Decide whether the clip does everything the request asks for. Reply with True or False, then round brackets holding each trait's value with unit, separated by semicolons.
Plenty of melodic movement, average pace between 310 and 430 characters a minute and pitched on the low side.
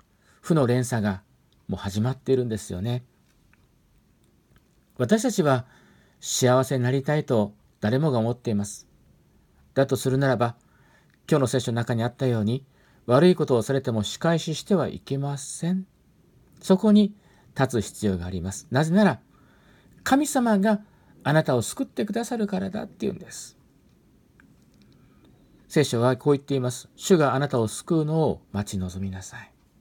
False (6.0 semitones; 300 characters per minute; 130 Hz)